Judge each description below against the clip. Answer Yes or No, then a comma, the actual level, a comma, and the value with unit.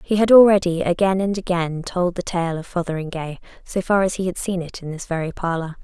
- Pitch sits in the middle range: Yes, medium, 180 Hz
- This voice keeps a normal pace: No, fast, 225 wpm